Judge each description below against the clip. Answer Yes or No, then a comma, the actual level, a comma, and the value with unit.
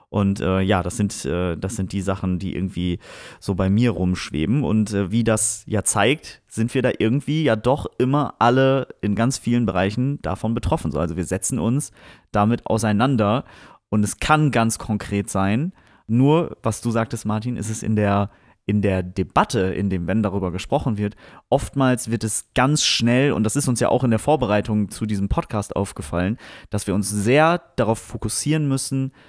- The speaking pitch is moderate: No, low, 110 Hz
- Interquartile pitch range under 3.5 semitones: No, average, 4.1 semitones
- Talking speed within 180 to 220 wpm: Yes, fast, 190 wpm